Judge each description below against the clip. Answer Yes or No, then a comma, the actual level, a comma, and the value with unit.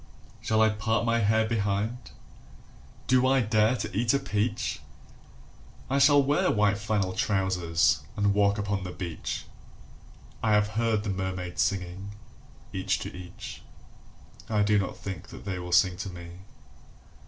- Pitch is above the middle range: No, low, 105 Hz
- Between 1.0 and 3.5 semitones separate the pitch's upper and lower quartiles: Yes, average, 2.8 semitones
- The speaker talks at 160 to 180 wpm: No, average, 145 wpm